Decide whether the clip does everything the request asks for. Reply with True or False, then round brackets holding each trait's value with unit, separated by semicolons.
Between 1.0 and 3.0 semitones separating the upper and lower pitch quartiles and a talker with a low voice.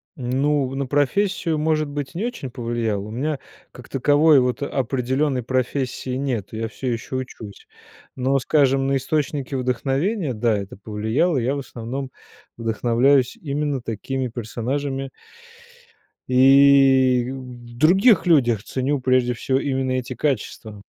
True (2.6 semitones; 130 Hz)